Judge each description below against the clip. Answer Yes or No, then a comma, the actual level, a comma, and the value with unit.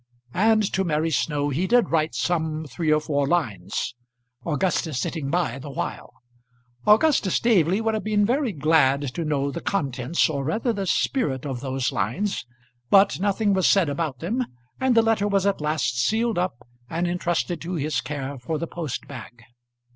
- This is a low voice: No, medium, 160 Hz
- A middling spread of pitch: No, wide, 6.0 semitones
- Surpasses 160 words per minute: Yes, average, 175 wpm